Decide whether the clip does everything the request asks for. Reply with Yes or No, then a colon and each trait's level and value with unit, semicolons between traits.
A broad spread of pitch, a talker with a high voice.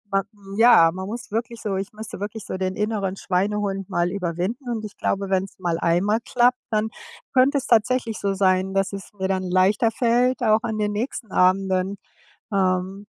No: average, 2.9 semitones; high, 200 Hz